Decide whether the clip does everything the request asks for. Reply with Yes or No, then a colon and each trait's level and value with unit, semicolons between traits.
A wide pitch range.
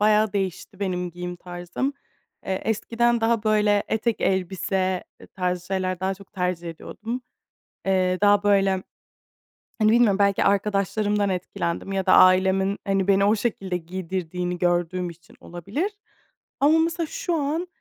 No: average, 2.7 semitones